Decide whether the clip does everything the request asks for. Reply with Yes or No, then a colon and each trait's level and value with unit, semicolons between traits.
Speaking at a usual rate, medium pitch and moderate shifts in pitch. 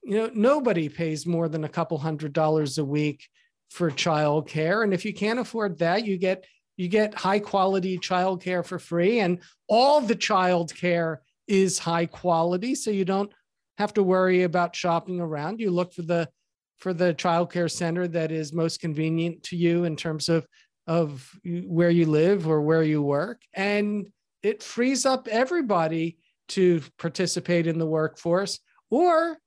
Yes: average, 175 wpm; medium, 175 Hz; average, 3.5 semitones